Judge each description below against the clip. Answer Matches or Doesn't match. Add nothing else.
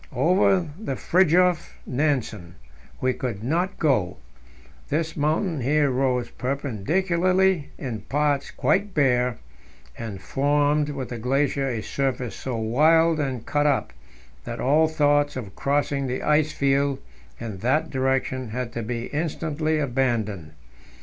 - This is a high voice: Doesn't match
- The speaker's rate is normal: Doesn't match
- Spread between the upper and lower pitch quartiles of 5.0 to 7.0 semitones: Doesn't match